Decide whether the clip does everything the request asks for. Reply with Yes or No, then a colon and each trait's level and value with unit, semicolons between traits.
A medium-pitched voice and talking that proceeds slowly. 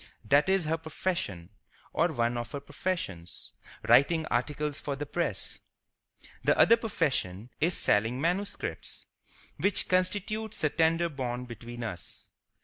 Yes: medium, 150 Hz; slow, 125 wpm